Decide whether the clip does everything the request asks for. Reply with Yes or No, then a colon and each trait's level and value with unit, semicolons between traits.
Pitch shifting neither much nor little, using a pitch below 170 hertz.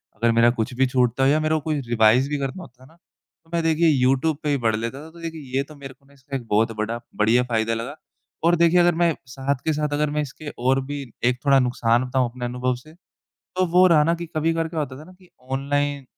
Yes: average, 4.0 semitones; medium, 140 Hz